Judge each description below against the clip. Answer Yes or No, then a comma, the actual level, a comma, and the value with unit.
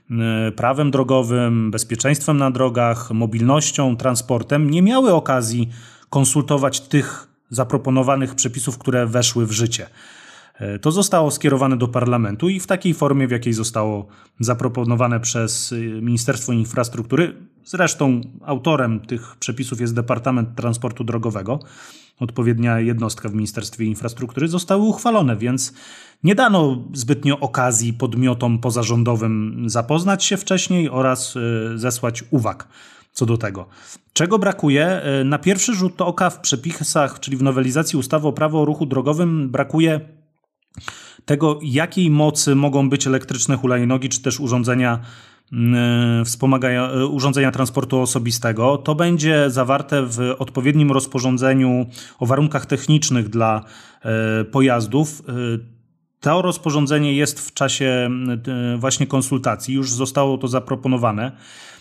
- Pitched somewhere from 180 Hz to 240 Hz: No, low, 130 Hz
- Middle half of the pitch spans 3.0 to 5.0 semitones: Yes, average, 3.5 semitones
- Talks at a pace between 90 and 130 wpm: Yes, average, 115 wpm